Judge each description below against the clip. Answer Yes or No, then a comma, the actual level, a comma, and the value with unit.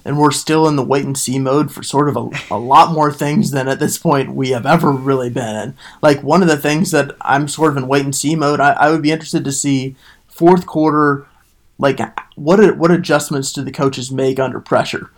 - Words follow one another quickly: Yes, fast, 240 wpm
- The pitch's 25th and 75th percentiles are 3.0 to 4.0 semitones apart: No, narrow, 2.5 semitones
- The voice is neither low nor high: Yes, medium, 145 Hz